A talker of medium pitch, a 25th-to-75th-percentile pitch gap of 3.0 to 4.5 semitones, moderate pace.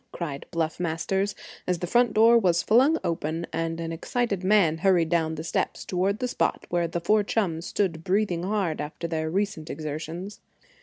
Yes: medium, 175 Hz; average, 3.8 semitones; average, 175 wpm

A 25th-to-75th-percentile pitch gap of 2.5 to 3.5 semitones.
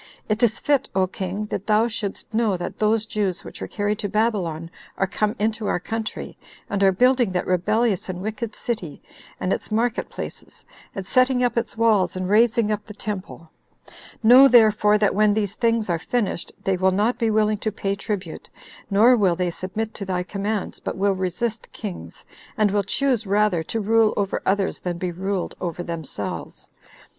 Yes: average, 2.9 semitones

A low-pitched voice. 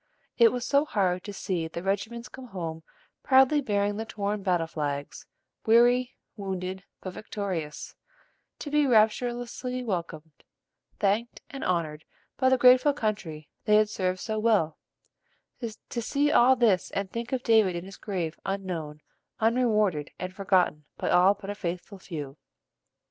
No: high, 200 Hz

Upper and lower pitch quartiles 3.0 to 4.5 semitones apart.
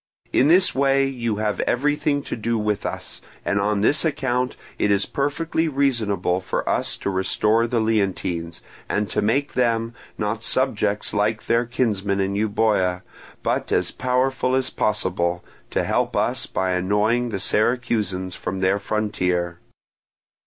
Yes: average, 4.2 semitones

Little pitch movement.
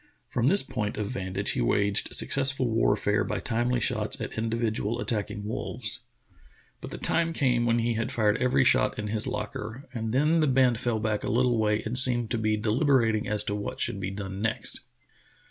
No: average, 3.1 semitones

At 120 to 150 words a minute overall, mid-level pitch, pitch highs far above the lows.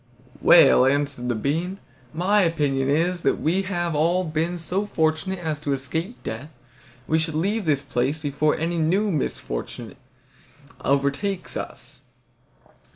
No: average, 140 wpm; medium, 160 Hz; average, 3.8 semitones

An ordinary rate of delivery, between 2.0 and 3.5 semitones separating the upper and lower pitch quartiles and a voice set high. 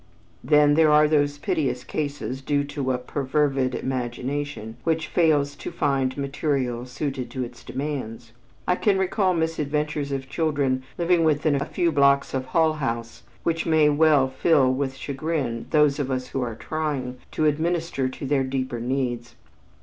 No: average, 155 wpm; average, 2.9 semitones; medium, 140 Hz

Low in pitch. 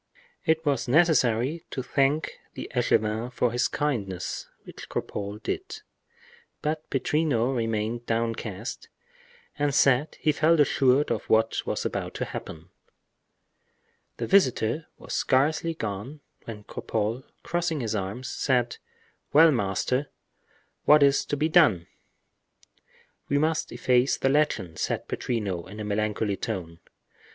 Yes: low, 125 Hz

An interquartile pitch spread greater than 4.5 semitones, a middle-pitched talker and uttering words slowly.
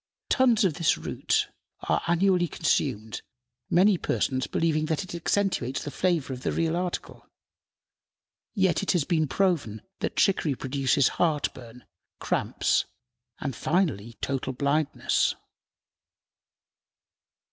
Yes: average, 5.0 semitones; medium, 155 Hz; slow, 115 wpm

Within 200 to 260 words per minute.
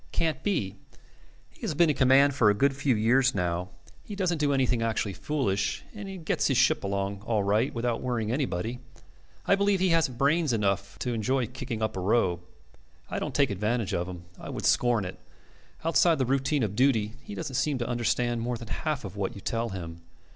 Yes: fast, 205 wpm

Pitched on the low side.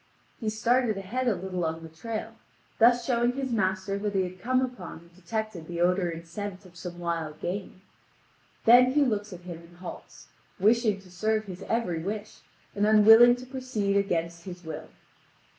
No: high, 200 Hz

